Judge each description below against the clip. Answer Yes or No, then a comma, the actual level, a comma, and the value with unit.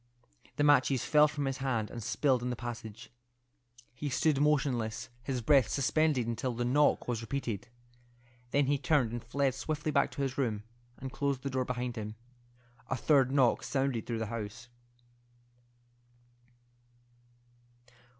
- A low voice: Yes, low, 130 Hz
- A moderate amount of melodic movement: Yes, average, 3.1 semitones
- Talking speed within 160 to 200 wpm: No, average, 150 wpm